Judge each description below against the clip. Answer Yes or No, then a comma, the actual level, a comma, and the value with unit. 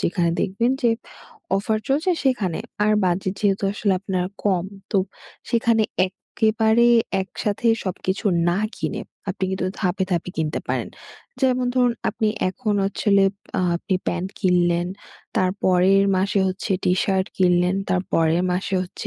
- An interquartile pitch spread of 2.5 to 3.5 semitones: Yes, average, 3.0 semitones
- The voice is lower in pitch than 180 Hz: No, high, 190 Hz